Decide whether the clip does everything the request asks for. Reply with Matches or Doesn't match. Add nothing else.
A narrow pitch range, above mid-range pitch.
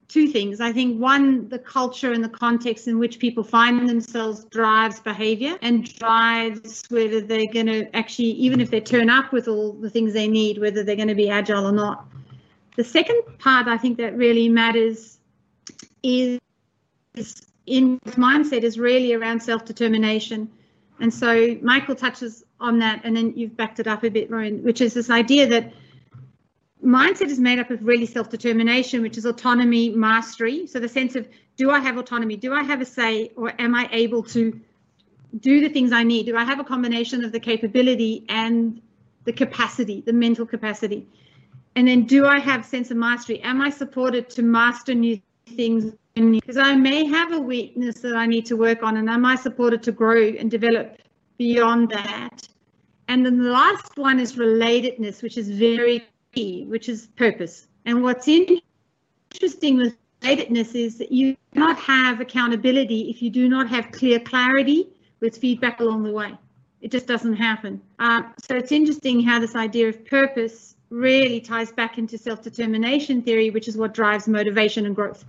Matches